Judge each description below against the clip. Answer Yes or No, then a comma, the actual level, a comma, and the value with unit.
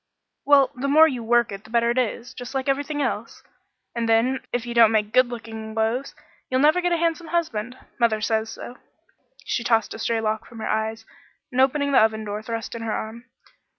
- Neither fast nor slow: No, fast, 215 wpm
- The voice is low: No, high, 235 Hz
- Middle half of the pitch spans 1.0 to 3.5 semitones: Yes, average, 3.1 semitones